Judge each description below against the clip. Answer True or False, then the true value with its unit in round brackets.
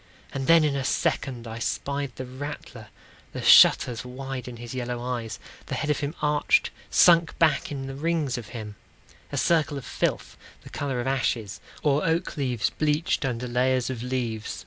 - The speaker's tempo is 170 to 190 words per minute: True (180 wpm)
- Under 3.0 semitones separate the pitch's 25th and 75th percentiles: False (3.3 semitones)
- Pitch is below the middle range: True (130 Hz)